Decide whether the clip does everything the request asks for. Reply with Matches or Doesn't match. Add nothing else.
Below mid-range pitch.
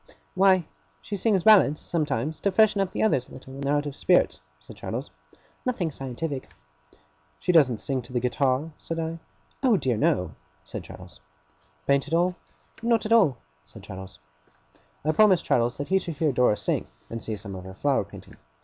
Doesn't match